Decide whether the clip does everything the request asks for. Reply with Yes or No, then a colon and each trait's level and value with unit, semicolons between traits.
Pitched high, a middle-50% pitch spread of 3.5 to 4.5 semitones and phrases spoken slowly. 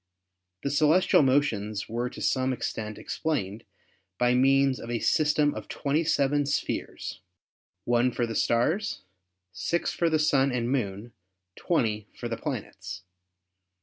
No: low, 130 Hz; average, 4.2 semitones; slow, 130 wpm